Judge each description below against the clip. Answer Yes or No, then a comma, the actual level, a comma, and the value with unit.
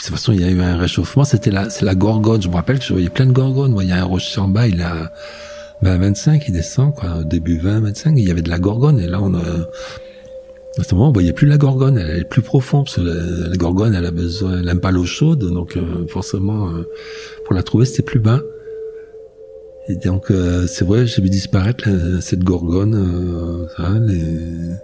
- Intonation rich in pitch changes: Yes, wide, 7.6 semitones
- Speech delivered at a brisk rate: Yes, fast, 245 wpm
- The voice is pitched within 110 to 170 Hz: No, low, 100 Hz